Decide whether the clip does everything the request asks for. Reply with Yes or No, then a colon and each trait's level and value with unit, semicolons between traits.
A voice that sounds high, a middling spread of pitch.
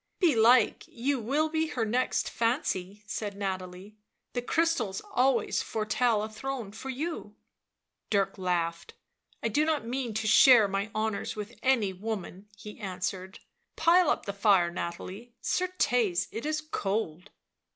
Yes: high, 220 Hz; average, 4.7 semitones